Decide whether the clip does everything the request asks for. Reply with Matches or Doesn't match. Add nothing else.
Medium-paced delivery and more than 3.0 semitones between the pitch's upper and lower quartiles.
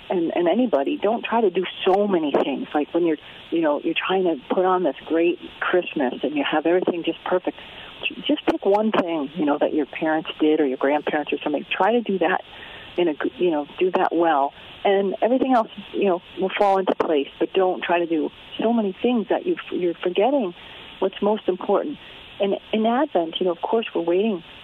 Doesn't match